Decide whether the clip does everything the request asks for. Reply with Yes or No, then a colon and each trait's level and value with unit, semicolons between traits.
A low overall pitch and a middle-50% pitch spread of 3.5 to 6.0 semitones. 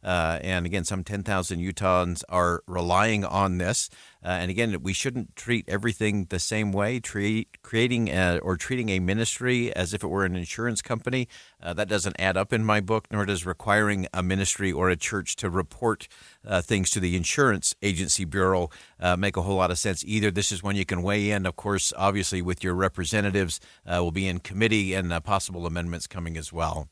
No: very low, 95 Hz; narrow, 2.5 semitones